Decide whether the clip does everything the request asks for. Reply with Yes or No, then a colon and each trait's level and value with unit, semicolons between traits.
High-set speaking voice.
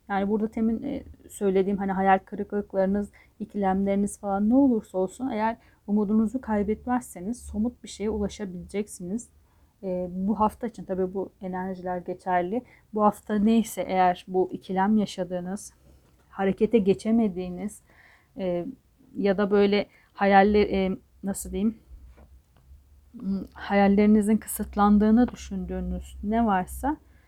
Yes: high, 200 Hz